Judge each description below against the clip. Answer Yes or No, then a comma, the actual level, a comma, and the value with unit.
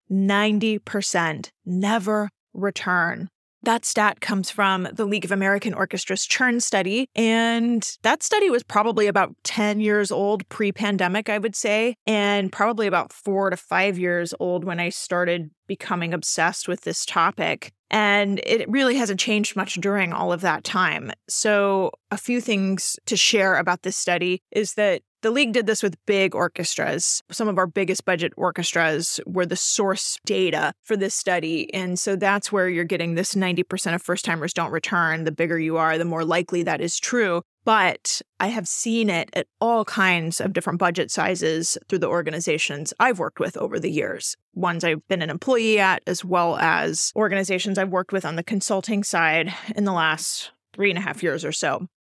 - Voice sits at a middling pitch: No, high, 195 Hz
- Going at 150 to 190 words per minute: Yes, average, 180 wpm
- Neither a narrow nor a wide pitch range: Yes, average, 3.1 semitones